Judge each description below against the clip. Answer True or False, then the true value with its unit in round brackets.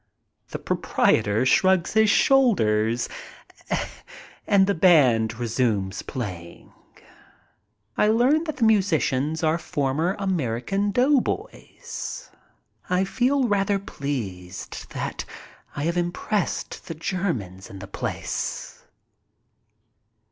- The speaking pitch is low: False (165 Hz)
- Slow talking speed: True (95 wpm)